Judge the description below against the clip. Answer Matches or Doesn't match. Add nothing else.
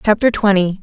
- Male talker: Doesn't match